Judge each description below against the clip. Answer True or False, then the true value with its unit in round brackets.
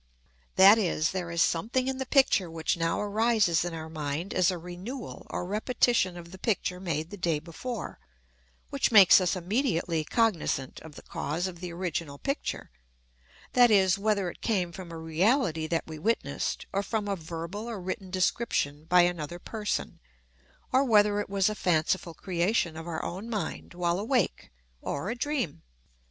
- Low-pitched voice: False (180 Hz)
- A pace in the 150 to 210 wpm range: True (170 wpm)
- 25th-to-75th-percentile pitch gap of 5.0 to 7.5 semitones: False (4.2 semitones)